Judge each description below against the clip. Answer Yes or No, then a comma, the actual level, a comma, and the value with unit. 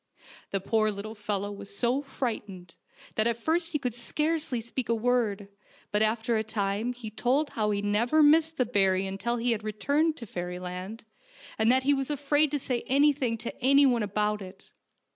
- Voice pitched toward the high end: Yes, high, 230 Hz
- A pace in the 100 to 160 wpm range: No, average, 180 wpm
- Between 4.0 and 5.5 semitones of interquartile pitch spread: Yes, average, 4.6 semitones